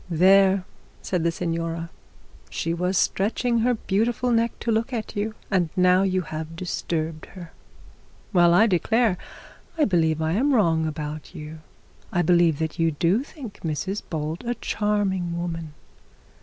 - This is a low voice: No, medium, 180 Hz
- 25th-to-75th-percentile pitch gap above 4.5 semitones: No, average, 4.2 semitones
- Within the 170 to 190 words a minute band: No, average, 150 wpm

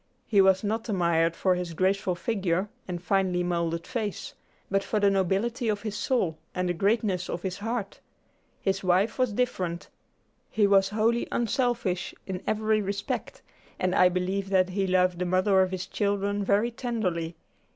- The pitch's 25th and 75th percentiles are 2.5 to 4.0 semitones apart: Yes, average, 2.8 semitones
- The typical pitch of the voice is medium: No, high, 195 Hz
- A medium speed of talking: Yes, average, 165 wpm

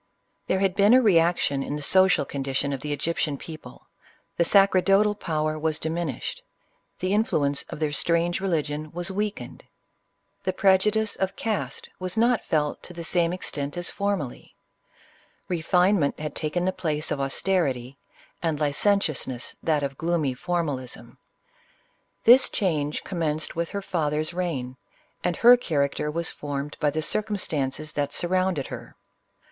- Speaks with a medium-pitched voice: Yes, medium, 165 Hz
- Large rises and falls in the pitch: No, average, 4.3 semitones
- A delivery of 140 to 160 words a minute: Yes, average, 150 wpm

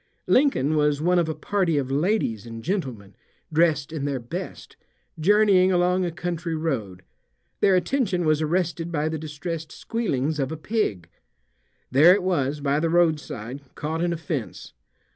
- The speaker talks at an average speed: Yes, average, 160 wpm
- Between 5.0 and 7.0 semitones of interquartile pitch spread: No, average, 3.9 semitones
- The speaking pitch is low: No, medium, 160 Hz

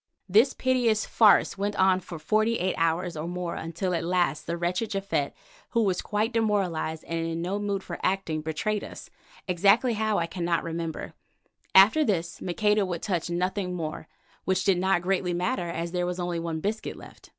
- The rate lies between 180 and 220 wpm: Yes, average, 185 wpm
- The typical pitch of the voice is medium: Yes, medium, 180 Hz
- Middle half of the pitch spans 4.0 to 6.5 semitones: No, average, 3.4 semitones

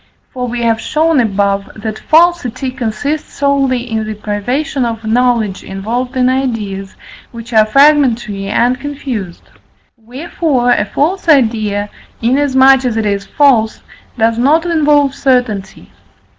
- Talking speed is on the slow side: Yes, slow, 130 wpm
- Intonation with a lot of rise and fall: No, average, 4.2 semitones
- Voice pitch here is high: Yes, high, 245 Hz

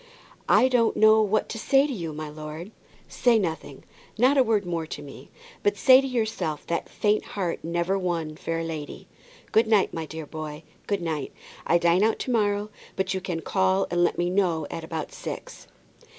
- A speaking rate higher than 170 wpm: Yes, average, 195 wpm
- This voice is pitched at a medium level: Yes, medium, 180 Hz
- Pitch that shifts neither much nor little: Yes, average, 5.0 semitones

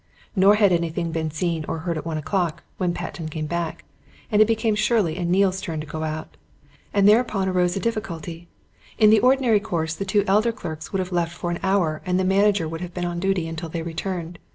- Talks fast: Yes, fast, 225 wpm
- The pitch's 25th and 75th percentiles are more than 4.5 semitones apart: No, average, 3.5 semitones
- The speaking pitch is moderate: Yes, medium, 175 Hz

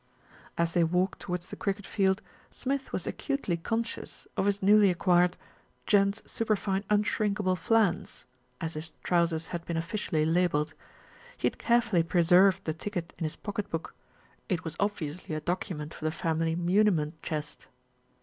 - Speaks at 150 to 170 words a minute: Yes, average, 155 wpm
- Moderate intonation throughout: Yes, average, 3.7 semitones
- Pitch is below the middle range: No, medium, 180 Hz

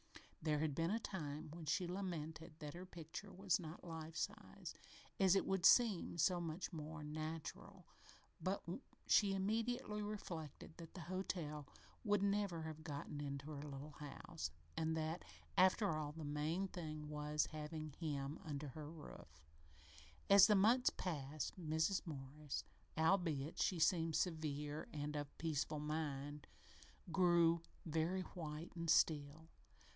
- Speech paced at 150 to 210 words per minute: No, average, 140 wpm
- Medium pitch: Yes, medium, 160 Hz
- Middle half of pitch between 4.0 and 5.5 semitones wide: No, average, 3.2 semitones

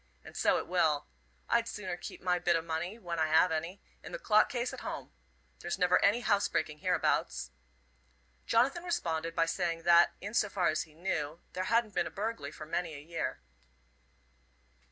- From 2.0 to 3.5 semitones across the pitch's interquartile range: No, average, 4.2 semitones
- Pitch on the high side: No, medium, 175 Hz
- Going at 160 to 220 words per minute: Yes, average, 185 wpm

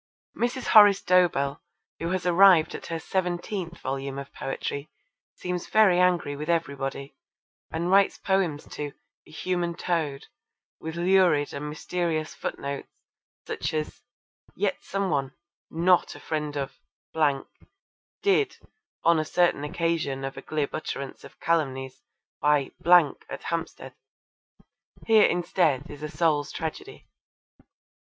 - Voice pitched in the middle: Yes, medium, 165 Hz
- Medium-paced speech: No, slow, 125 wpm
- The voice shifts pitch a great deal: No, average, 3.8 semitones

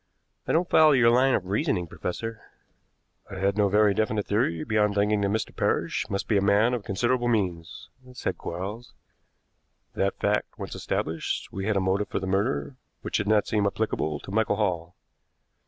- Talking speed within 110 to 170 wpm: No, average, 180 wpm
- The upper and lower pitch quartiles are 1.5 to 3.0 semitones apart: Yes, narrow, 2.4 semitones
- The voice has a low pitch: Yes, low, 105 Hz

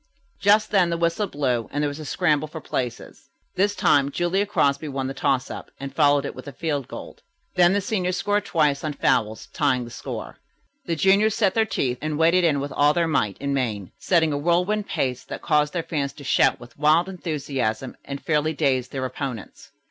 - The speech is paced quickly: Yes, fast, 210 wpm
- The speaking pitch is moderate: Yes, medium, 150 Hz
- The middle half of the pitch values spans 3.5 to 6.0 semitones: Yes, average, 4.3 semitones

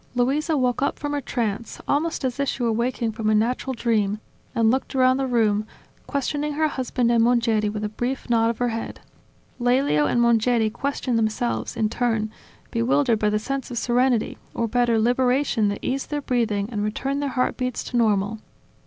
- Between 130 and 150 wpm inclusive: No, average, 190 wpm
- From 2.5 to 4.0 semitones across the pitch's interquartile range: Yes, average, 3.1 semitones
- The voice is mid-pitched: No, high, 240 Hz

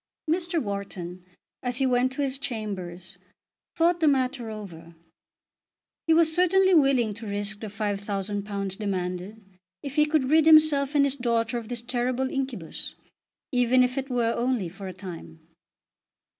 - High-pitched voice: Yes, high, 240 Hz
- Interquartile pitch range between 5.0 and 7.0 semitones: Yes, wide, 5.5 semitones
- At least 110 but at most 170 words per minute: Yes, average, 150 wpm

